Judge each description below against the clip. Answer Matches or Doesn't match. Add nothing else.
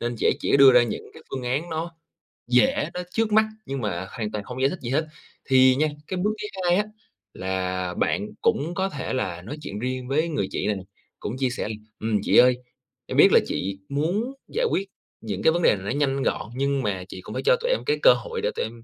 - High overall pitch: Doesn't match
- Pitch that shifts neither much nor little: Doesn't match